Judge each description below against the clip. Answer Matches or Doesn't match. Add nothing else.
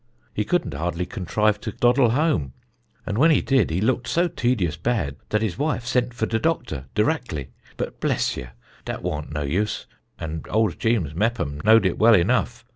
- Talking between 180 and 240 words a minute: Matches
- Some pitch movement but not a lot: Doesn't match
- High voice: Doesn't match